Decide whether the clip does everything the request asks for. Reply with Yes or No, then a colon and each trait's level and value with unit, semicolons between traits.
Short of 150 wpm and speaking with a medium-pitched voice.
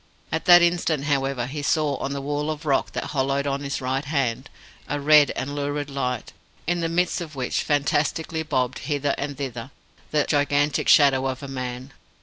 No: average, 185 wpm; medium, 145 Hz